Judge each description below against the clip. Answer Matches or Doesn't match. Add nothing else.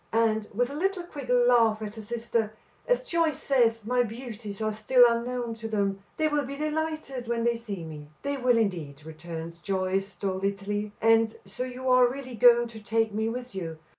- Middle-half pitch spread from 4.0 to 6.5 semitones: Doesn't match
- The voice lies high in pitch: Matches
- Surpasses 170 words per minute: Matches